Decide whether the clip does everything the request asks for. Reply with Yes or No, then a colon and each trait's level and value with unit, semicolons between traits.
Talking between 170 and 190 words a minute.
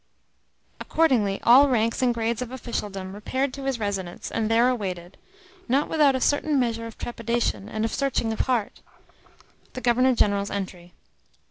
No: average, 155 wpm